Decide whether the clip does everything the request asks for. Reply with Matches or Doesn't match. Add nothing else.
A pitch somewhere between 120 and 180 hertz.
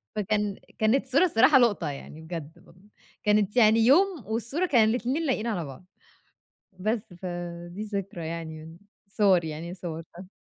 Doesn't match